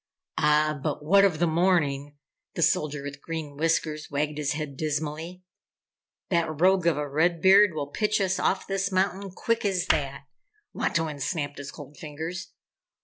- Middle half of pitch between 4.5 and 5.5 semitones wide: No, average, 3.7 semitones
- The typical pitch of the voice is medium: Yes, medium, 155 Hz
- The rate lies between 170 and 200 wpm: No, average, 160 wpm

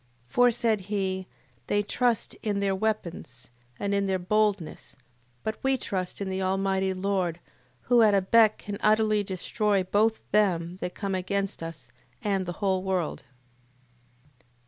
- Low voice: No, high, 195 Hz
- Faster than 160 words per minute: No, average, 150 wpm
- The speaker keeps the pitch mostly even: Yes, narrow, 2.2 semitones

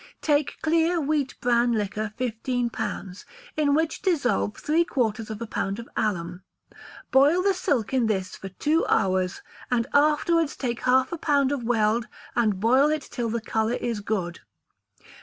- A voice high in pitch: Yes, high, 245 Hz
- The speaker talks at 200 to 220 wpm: No, average, 160 wpm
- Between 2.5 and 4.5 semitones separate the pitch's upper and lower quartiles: No, wide, 5.4 semitones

